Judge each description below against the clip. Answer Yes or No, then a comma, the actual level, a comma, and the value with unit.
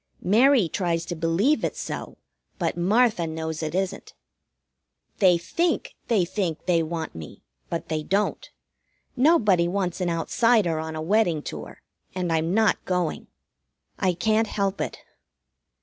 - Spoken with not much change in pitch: No, average, 4.2 semitones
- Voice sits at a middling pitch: Yes, medium, 180 Hz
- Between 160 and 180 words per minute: No, average, 140 wpm